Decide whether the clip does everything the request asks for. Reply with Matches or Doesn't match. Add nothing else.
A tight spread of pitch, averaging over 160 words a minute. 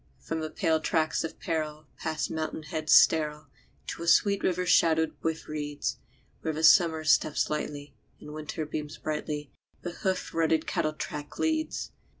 Doesn't match